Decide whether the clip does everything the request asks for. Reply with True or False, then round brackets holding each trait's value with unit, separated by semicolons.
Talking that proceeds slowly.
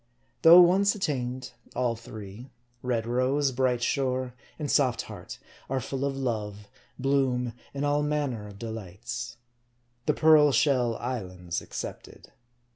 True (130 wpm)